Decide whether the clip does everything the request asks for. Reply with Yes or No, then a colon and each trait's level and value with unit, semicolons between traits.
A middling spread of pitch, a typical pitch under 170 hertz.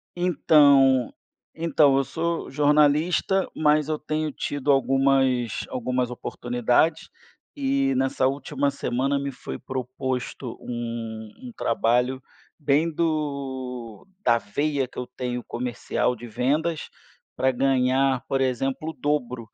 Yes: average, 3.3 semitones; low, 135 Hz